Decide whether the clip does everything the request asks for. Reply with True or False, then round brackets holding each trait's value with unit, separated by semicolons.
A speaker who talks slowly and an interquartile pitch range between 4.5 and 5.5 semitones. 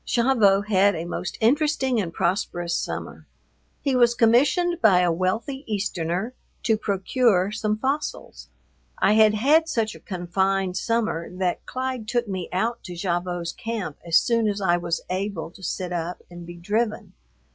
False (155 wpm; 4.8 semitones)